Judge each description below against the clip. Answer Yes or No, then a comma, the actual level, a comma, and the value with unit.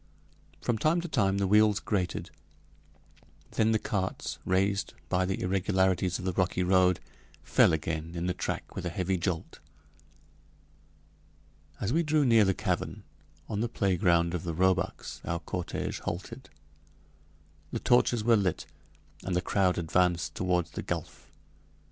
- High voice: No, very low, 95 Hz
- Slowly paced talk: No, average, 145 wpm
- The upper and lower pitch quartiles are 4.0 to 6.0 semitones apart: No, average, 2.7 semitones